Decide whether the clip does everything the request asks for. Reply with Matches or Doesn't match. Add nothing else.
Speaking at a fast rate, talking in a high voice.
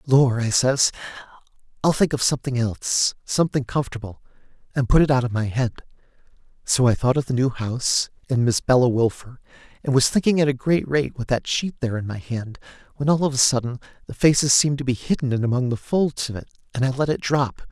Doesn't match